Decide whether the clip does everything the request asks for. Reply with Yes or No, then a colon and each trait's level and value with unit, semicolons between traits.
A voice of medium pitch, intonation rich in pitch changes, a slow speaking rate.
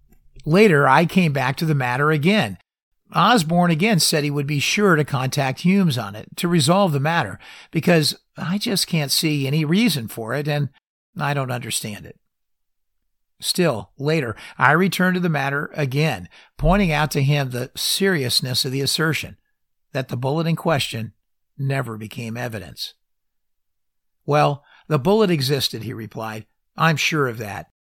No: medium, 145 Hz; wide, 5.9 semitones; average, 155 wpm